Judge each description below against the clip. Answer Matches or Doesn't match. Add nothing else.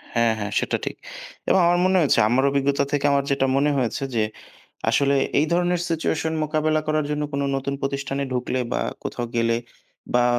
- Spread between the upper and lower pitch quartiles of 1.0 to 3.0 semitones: Matches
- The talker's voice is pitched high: Doesn't match